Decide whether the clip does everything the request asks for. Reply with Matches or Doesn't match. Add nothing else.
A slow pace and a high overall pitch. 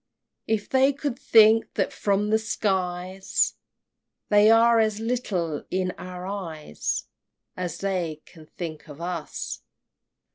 Matches